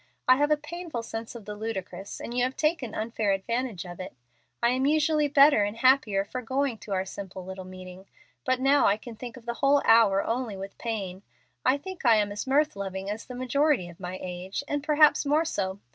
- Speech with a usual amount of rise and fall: No, wide, 6.0 semitones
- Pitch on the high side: Yes, high, 230 Hz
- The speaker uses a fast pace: Yes, fast, 220 wpm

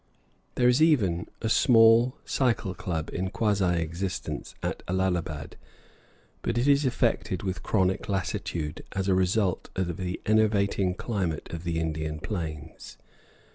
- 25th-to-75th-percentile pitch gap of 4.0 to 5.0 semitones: Yes, average, 4.4 semitones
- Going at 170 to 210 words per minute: No, slow, 135 wpm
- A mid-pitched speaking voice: No, very low, 95 Hz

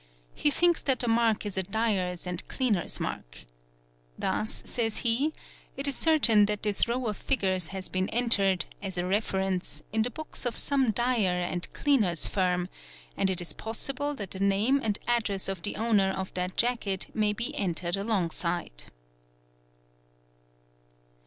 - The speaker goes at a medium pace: Yes, average, 160 wpm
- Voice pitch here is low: No, high, 205 Hz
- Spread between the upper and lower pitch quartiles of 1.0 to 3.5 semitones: No, average, 4.2 semitones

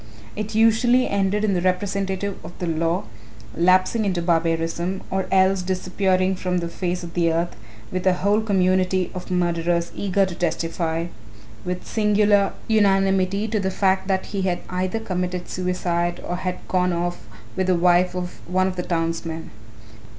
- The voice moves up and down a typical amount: No, narrow, 1.8 semitones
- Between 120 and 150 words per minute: No, average, 160 wpm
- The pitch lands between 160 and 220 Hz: Yes, medium, 185 Hz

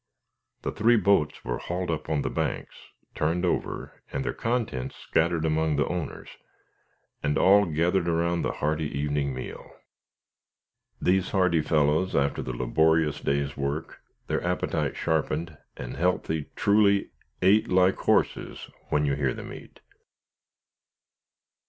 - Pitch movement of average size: Yes, average, 3.7 semitones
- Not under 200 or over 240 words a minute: No, slow, 135 wpm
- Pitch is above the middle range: No, very low, 80 Hz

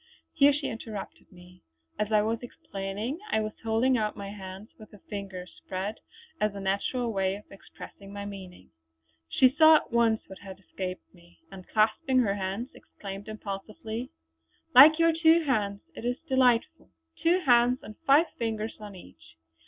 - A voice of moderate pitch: No, high, 215 Hz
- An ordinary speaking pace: Yes, average, 165 wpm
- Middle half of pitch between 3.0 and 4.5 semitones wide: Yes, average, 4.1 semitones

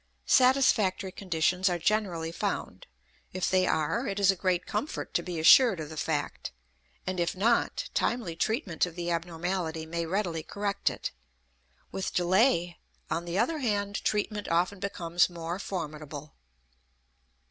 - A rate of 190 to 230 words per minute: No, average, 145 wpm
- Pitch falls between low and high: Yes, medium, 180 Hz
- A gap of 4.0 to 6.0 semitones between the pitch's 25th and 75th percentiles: No, average, 3.3 semitones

